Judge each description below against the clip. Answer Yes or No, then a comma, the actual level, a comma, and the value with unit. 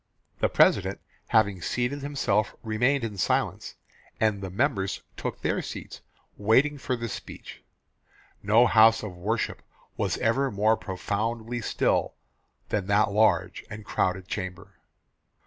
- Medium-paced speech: No, slow, 130 wpm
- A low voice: Yes, low, 110 Hz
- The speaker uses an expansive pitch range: No, average, 2.8 semitones